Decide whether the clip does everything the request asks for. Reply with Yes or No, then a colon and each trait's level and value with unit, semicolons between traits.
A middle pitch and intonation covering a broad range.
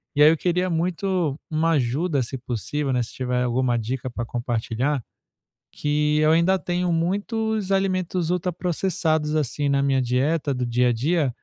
Yes: medium, 150 Hz; wide, 5.8 semitones